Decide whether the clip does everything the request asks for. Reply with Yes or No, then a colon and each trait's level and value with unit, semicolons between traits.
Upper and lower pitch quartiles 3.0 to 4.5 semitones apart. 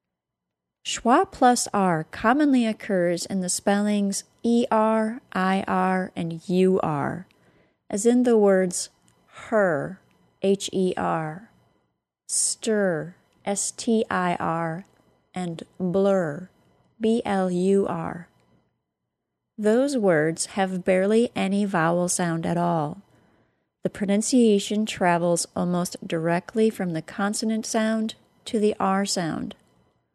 Yes: average, 3.8 semitones